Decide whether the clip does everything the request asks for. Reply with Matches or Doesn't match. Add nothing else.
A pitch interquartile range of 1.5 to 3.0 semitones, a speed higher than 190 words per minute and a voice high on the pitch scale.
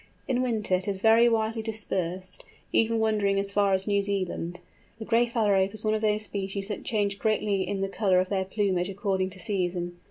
Matches